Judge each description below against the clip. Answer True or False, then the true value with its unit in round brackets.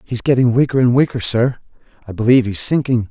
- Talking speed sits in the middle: True (195 wpm)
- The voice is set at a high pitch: False (120 Hz)